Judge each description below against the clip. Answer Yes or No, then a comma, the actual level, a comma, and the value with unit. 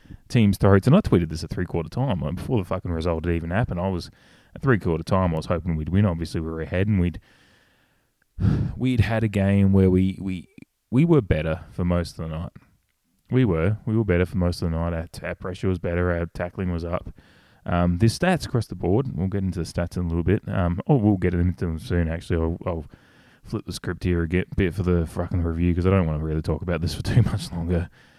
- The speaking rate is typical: No, fast, 245 wpm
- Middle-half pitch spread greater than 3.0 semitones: No, average, 2.7 semitones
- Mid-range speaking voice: No, very low, 90 Hz